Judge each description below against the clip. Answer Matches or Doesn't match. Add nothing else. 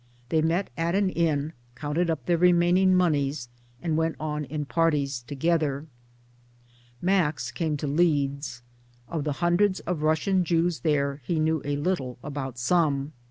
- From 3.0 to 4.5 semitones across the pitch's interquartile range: Matches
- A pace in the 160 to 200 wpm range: Doesn't match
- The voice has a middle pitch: Matches